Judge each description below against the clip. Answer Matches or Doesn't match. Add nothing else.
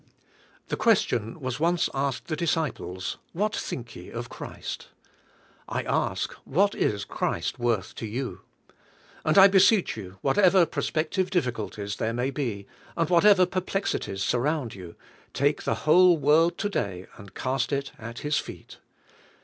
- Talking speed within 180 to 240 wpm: Doesn't match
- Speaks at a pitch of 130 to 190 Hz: Matches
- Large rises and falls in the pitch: Matches